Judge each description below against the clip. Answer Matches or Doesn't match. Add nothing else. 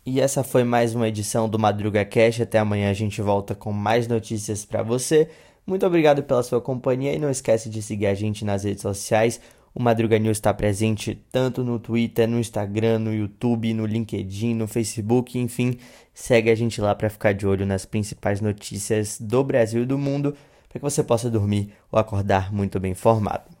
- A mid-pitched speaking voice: Doesn't match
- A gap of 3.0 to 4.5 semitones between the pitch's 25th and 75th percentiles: Doesn't match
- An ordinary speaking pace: Doesn't match